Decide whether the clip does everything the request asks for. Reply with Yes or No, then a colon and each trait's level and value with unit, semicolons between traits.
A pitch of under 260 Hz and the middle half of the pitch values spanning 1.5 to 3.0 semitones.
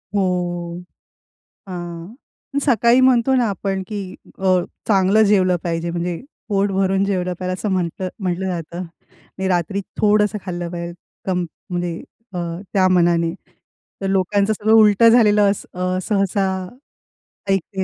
Yes: high, 190 Hz; narrow, 2.5 semitones